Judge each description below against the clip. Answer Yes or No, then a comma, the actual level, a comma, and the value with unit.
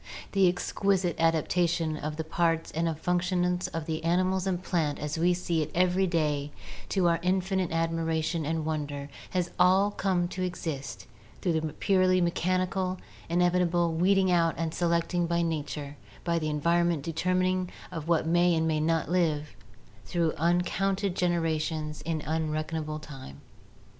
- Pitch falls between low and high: Yes, medium, 170 Hz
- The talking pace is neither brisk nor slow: Yes, average, 150 wpm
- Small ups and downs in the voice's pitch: Yes, narrow, 2.2 semitones